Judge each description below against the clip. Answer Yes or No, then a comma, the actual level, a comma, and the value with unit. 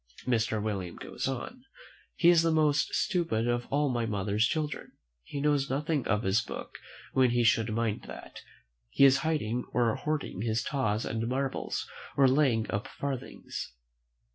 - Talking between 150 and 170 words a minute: Yes, average, 160 wpm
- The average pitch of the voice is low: Yes, low, 125 Hz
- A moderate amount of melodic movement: Yes, average, 4.6 semitones